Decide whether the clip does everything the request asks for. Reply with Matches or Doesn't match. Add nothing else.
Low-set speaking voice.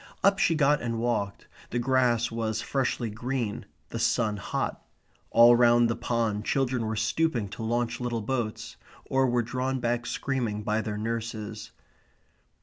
Matches